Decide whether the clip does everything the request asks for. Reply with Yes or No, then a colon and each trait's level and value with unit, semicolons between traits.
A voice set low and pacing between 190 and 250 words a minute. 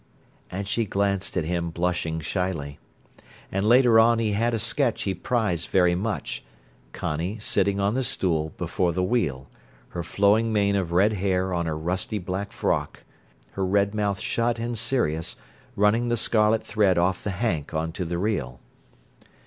No: low, 100 Hz; average, 165 wpm